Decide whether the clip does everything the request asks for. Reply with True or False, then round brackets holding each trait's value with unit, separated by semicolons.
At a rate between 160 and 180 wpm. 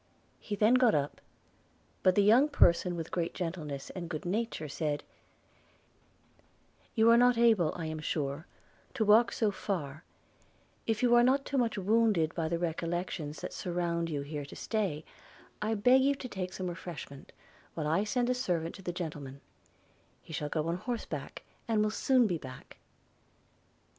True (170 wpm)